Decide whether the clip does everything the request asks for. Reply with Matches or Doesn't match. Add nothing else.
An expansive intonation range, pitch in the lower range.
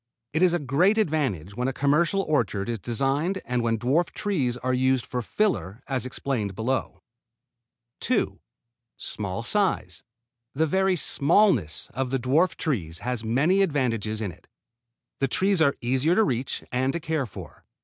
Matches